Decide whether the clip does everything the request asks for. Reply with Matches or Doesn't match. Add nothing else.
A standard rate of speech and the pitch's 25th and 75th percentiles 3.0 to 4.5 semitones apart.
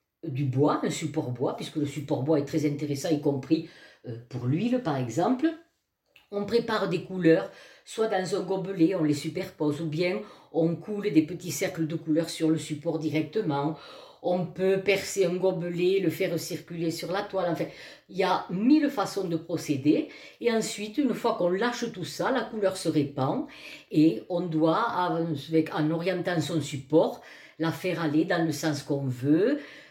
Matches